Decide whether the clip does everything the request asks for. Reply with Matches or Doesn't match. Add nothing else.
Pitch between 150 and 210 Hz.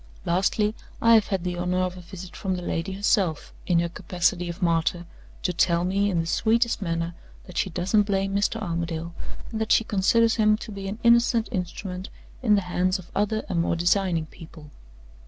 Matches